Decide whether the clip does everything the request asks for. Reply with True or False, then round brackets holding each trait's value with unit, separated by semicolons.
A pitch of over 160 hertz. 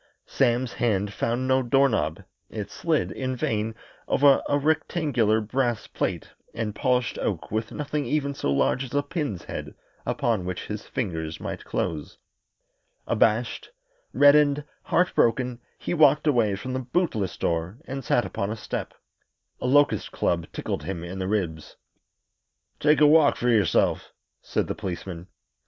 False (120 Hz)